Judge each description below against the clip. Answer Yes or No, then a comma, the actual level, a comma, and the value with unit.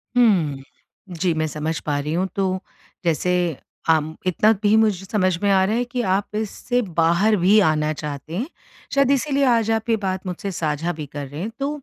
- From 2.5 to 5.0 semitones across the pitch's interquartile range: No, wide, 5.6 semitones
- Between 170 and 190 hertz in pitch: Yes, medium, 185 Hz